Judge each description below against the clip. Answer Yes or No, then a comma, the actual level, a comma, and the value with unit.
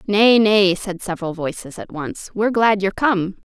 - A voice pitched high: Yes, high, 200 Hz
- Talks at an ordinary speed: Yes, average, 190 wpm